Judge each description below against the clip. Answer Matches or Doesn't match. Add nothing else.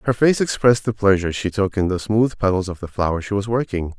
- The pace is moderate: Doesn't match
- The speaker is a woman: Doesn't match